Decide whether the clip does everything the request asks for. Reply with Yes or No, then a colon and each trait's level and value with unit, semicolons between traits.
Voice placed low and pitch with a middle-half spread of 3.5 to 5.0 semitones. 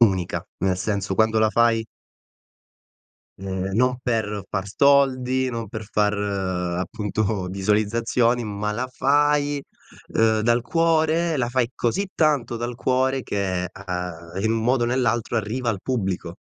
Yes: low, 115 Hz; average, 4.0 semitones